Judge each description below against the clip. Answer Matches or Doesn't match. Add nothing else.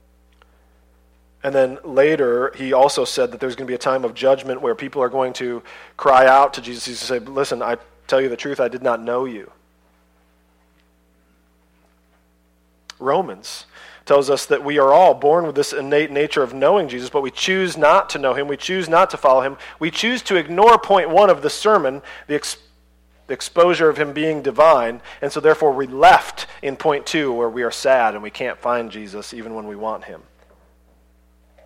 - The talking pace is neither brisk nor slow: Matches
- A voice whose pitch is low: Matches